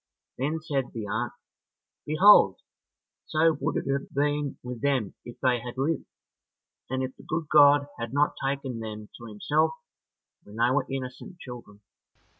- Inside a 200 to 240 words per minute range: No, average, 155 wpm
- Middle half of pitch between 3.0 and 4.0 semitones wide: Yes, average, 3.5 semitones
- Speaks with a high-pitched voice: No, low, 135 Hz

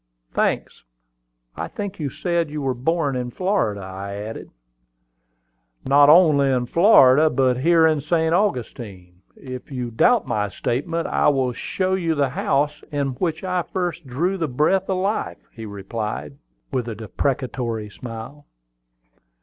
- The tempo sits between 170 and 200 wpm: No, average, 145 wpm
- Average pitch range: No, wide, 5.8 semitones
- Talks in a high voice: No, medium, 140 Hz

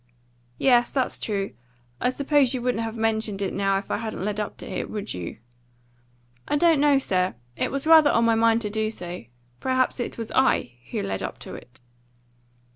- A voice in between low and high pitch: No, high, 225 Hz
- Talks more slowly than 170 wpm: No, average, 200 wpm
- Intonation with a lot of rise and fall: No, average, 4.6 semitones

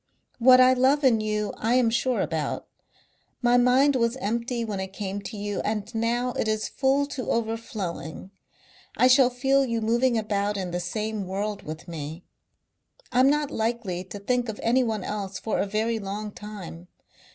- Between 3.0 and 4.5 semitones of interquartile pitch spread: Yes, average, 3.6 semitones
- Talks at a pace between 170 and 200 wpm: Yes, average, 175 wpm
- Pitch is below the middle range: No, high, 220 Hz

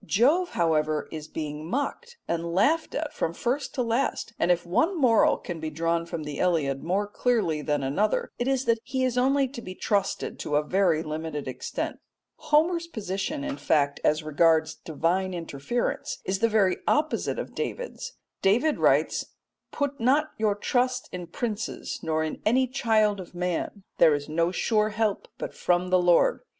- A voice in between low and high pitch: No, high, 195 Hz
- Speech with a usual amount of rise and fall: No, wide, 7.4 semitones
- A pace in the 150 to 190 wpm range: Yes, average, 175 wpm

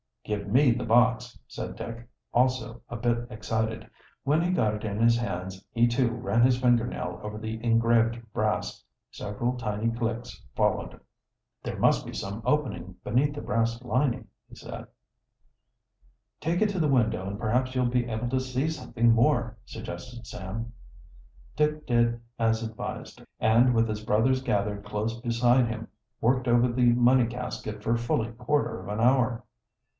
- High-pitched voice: No, low, 120 Hz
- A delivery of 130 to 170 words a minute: Yes, average, 160 wpm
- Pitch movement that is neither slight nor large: No, narrow, 2.1 semitones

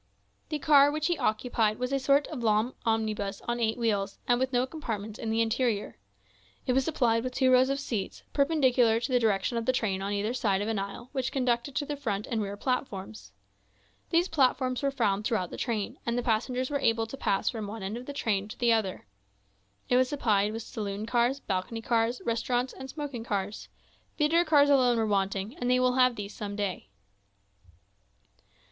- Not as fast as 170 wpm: No, fast, 205 wpm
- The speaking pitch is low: No, high, 235 Hz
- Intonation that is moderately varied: Yes, average, 3.6 semitones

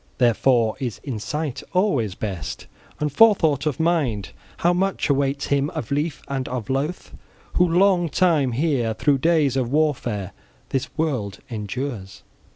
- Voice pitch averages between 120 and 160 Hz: Yes, medium, 140 Hz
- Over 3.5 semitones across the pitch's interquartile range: Yes, average, 5.1 semitones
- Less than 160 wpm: Yes, average, 140 wpm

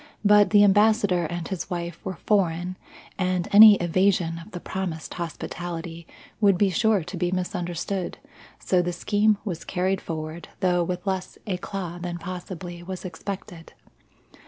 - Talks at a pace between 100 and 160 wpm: Yes, average, 145 wpm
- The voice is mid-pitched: Yes, medium, 180 Hz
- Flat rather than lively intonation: Yes, narrow, 2.2 semitones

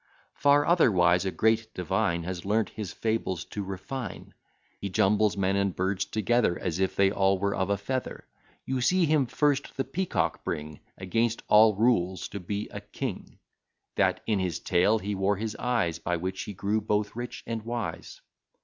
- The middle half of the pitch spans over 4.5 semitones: No, average, 3.6 semitones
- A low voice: Yes, low, 100 Hz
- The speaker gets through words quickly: No, average, 175 wpm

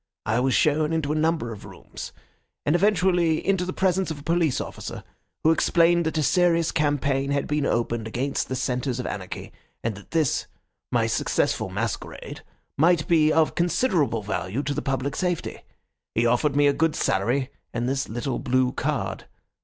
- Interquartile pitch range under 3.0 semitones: No, average, 4.8 semitones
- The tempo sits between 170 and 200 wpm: Yes, average, 175 wpm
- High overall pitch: No, medium, 145 Hz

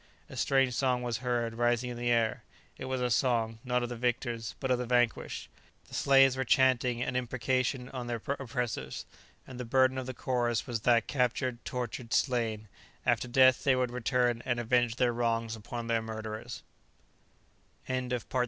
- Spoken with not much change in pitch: Yes, narrow, 1.6 semitones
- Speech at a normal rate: Yes, average, 170 wpm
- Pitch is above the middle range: No, low, 120 Hz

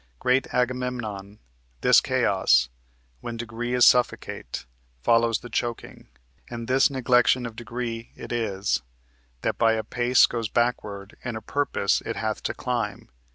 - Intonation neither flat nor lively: No, narrow, 2.0 semitones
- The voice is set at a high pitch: No, low, 120 Hz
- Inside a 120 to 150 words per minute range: Yes, average, 140 wpm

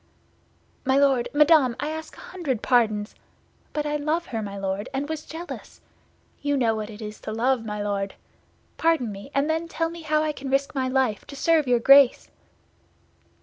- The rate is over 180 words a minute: Yes, average, 190 wpm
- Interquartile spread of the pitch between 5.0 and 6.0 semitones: Yes, wide, 5.4 semitones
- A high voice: Yes, very high, 270 Hz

